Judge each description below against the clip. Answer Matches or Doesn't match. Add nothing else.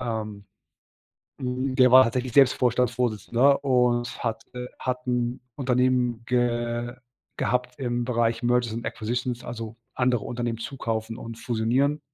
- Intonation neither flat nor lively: Doesn't match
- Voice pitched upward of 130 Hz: Doesn't match